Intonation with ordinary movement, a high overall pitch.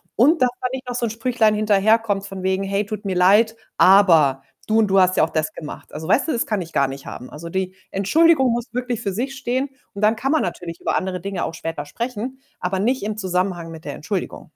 Yes: average, 4.6 semitones; high, 200 Hz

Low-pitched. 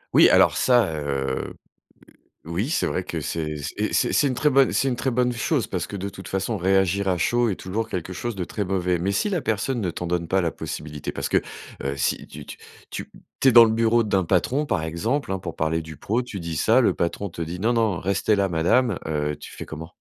Yes: very low, 95 Hz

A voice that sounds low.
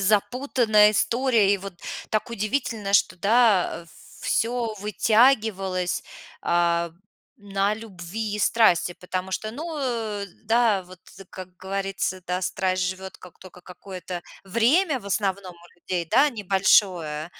No: high, 200 Hz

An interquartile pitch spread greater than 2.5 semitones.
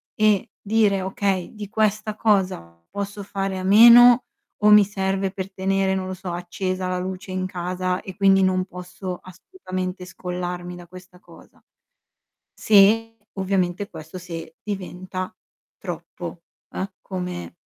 No: narrow, 1.8 semitones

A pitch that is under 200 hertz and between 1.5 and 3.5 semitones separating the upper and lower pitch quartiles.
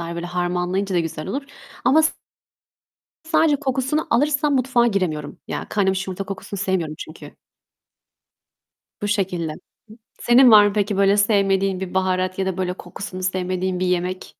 Yes: high, 190 Hz; average, 2.9 semitones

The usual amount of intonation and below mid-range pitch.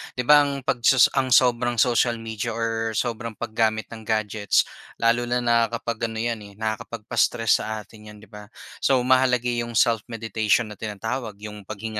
No: narrow, 1.8 semitones; low, 115 Hz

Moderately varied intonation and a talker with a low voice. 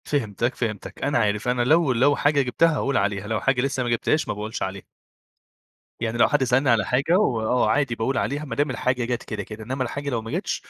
Yes: average, 3.8 semitones; low, 125 Hz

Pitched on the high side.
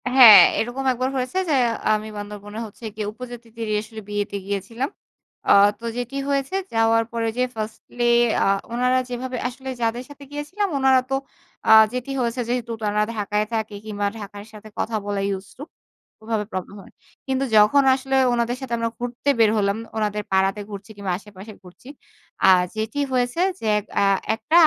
Yes: high, 225 Hz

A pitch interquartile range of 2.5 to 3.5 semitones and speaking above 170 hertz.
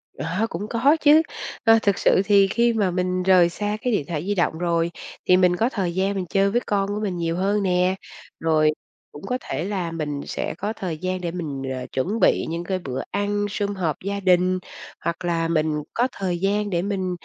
Yes: average, 3.1 semitones; medium, 185 Hz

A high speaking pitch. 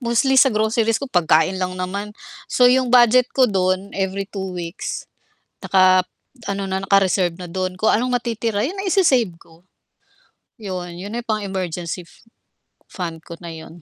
Yes: high, 195 Hz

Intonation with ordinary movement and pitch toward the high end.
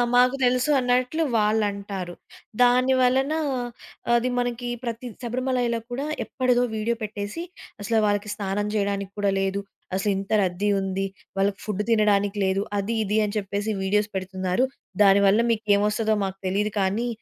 Yes: average, 3.5 semitones; high, 210 Hz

